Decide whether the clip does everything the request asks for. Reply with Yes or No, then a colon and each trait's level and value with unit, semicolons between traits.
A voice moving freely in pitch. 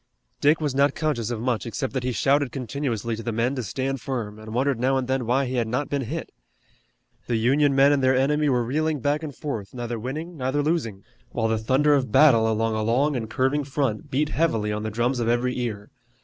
No: average, 3.8 semitones